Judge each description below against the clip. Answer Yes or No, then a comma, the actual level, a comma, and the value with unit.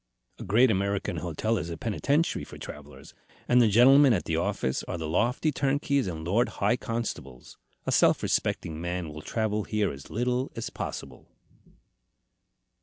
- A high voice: No, low, 105 Hz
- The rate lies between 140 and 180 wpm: Yes, average, 160 wpm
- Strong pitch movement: Yes, wide, 6.5 semitones